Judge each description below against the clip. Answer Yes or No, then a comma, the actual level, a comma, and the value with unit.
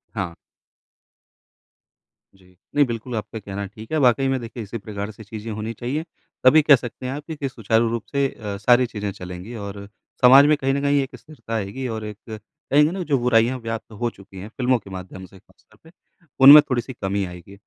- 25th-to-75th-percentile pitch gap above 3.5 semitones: Yes, average, 4.7 semitones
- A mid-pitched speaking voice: No, low, 115 Hz